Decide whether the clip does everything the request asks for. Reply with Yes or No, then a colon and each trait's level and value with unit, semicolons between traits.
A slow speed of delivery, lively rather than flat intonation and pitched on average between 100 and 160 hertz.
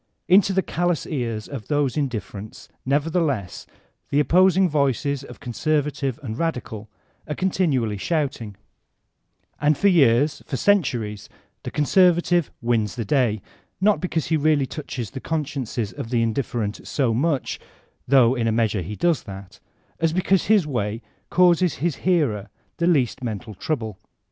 No: average, 150 wpm; wide, 6.3 semitones; medium, 140 Hz